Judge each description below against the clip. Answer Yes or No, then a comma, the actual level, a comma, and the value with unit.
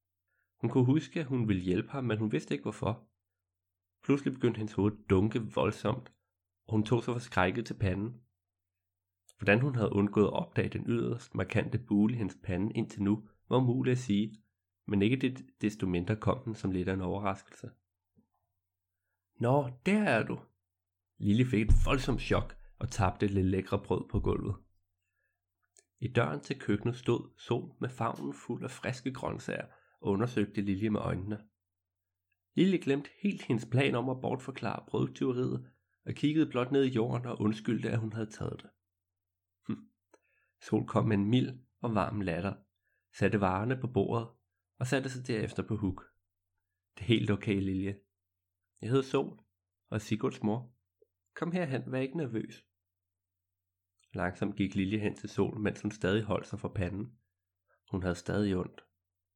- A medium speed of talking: Yes, average, 170 wpm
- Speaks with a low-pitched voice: Yes, low, 100 Hz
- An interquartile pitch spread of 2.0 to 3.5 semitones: No, average, 4.5 semitones